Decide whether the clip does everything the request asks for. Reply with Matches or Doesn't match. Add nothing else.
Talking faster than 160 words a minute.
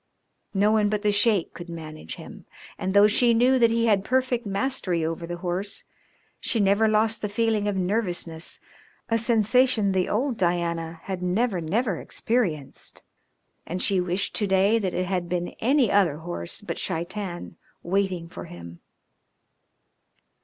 Doesn't match